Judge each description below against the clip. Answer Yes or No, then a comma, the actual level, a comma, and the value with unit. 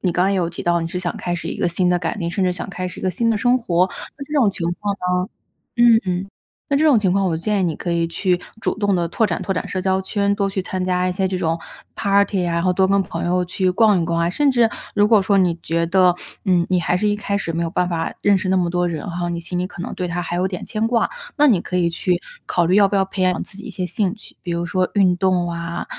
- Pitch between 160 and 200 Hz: Yes, medium, 185 Hz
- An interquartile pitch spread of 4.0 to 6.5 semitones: No, narrow, 2.5 semitones